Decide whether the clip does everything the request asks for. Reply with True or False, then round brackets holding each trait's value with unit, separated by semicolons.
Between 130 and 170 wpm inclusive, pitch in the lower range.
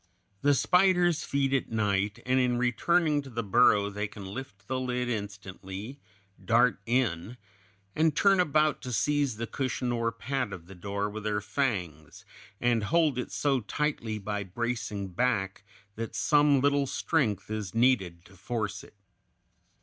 True (155 wpm; 115 Hz)